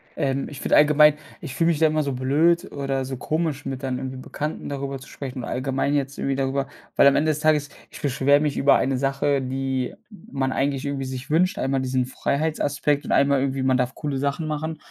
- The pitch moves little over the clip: Yes, narrow, 1.9 semitones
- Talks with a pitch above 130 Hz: Yes, medium, 140 Hz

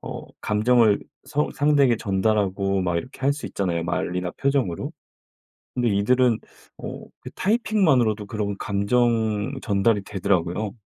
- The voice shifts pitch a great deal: No, average, 4.3 semitones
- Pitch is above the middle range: No, low, 105 Hz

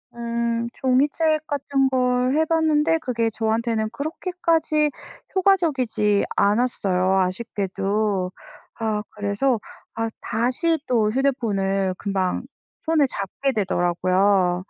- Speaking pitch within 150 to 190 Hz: No, high, 235 Hz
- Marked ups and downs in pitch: Yes, wide, 6.0 semitones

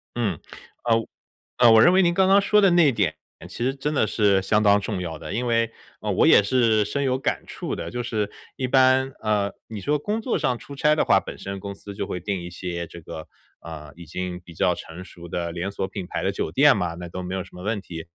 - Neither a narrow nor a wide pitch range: No, wide, 6.3 semitones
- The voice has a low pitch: Yes, low, 105 Hz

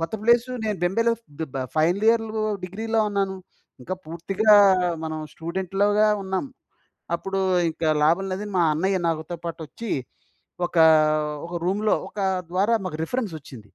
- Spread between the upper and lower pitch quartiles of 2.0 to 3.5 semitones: No, average, 4.2 semitones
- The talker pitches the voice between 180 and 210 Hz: Yes, high, 190 Hz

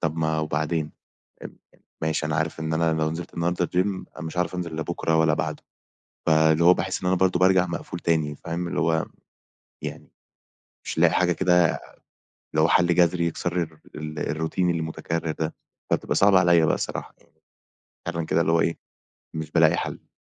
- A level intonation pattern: Yes, narrow, 1.7 semitones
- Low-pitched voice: Yes, very low, 80 Hz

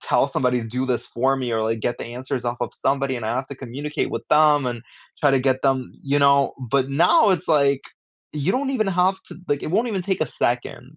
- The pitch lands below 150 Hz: Yes, low, 135 Hz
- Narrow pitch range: No, average, 3.4 semitones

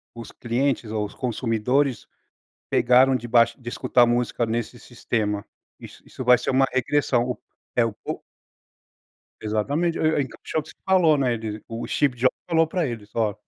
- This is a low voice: Yes, low, 120 Hz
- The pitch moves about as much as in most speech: Yes, average, 3.0 semitones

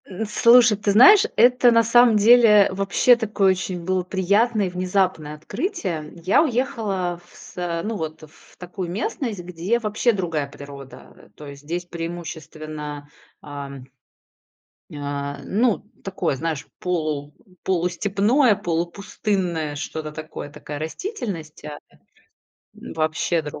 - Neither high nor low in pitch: Yes, medium, 180 Hz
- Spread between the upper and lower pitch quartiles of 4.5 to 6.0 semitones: Yes, wide, 5.4 semitones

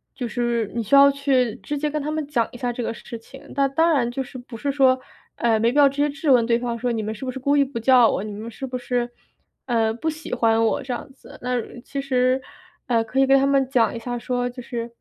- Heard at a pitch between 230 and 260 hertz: Yes, very high, 250 Hz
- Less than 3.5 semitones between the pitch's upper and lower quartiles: Yes, average, 2.7 semitones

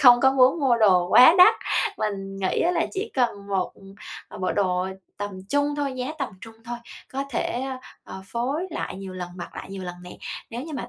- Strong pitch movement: Yes, wide, 5.8 semitones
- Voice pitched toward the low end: No, high, 235 Hz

